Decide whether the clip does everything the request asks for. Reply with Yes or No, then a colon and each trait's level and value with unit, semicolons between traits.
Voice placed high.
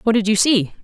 Yes: high, 215 Hz